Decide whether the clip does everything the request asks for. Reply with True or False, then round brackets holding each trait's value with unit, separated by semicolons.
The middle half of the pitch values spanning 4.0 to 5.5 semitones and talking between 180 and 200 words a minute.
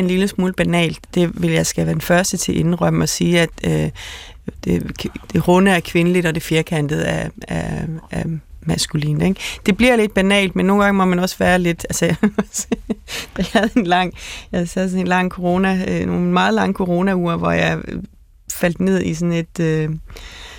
False (2.8 semitones; 190 wpm)